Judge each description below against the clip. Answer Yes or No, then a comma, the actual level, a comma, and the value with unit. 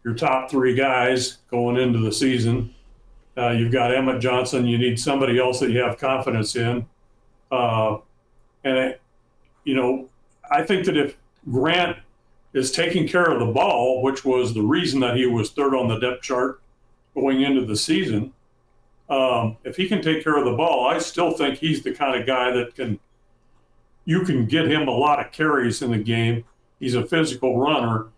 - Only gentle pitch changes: Yes, narrow, 2.2 semitones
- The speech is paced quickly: No, average, 185 wpm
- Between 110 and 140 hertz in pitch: Yes, low, 125 Hz